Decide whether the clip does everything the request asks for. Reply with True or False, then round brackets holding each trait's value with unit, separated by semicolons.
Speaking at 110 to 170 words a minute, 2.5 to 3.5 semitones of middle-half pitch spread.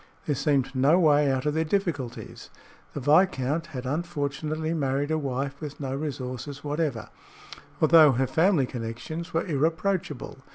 True (140 wpm; 3.1 semitones)